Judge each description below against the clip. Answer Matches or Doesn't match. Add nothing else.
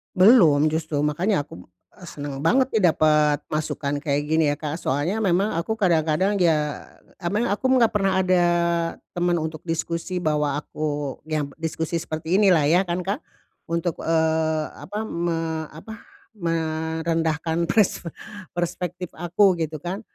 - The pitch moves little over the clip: Doesn't match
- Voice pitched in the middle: Matches